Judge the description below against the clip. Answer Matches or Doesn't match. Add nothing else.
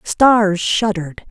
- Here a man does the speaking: Doesn't match